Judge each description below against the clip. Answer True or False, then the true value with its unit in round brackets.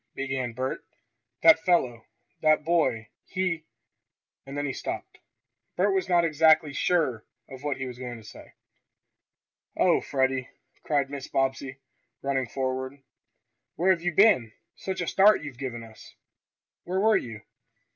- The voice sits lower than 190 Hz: True (140 Hz)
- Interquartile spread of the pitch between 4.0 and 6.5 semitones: True (4.8 semitones)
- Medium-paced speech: True (150 wpm)